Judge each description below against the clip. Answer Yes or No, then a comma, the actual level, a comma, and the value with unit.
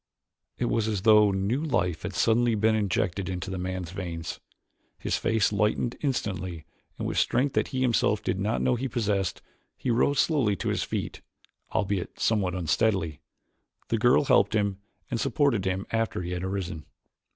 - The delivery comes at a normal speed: Yes, average, 170 wpm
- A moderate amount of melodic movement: Yes, average, 3.8 semitones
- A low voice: Yes, low, 105 Hz